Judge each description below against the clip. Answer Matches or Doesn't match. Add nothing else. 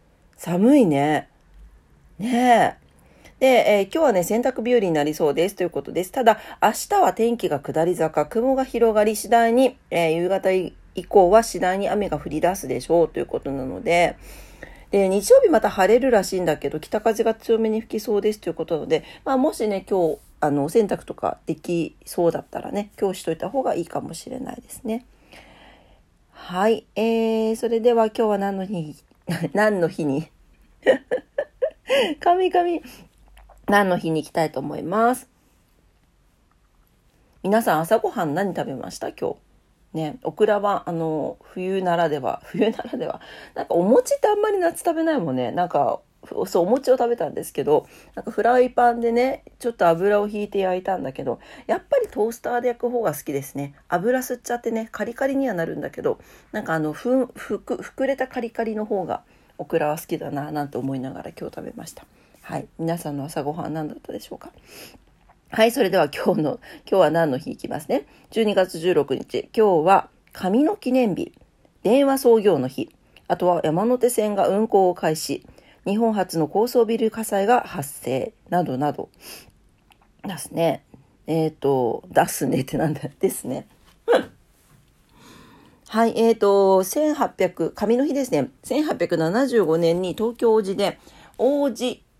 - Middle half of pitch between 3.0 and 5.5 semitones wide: Doesn't match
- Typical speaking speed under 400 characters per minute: Matches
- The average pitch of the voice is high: Matches